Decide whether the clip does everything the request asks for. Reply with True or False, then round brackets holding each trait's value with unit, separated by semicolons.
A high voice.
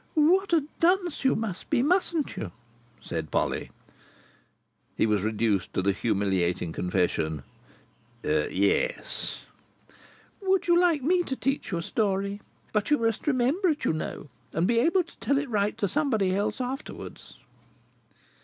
True (225 Hz)